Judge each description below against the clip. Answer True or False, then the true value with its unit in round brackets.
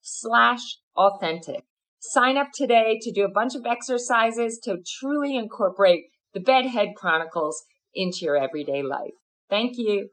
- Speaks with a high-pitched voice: True (220 Hz)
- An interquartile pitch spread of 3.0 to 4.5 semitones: False (4.9 semitones)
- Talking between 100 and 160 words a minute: True (135 wpm)